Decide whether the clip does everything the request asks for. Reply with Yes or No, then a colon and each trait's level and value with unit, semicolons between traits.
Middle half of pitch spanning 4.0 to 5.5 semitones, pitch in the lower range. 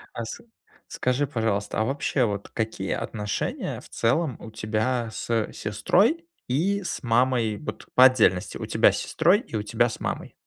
Yes: average, 4.4 semitones; low, 115 Hz